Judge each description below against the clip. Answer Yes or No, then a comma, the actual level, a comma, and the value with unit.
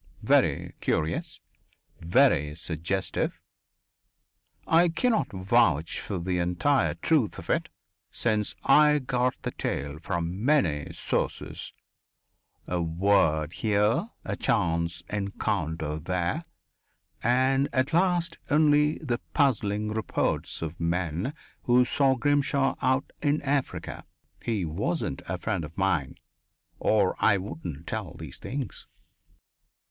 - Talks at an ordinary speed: No, slow, 110 wpm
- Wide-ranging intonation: Yes, wide, 8.3 semitones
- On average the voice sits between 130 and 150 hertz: No, low, 100 Hz